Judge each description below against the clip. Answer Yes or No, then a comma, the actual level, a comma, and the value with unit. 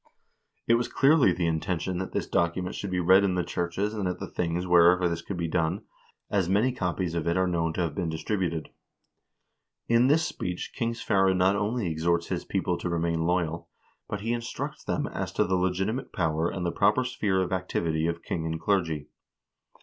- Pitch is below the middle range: Yes, very low, 90 Hz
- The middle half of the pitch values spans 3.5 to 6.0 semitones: No, average, 2.9 semitones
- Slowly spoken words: No, average, 200 wpm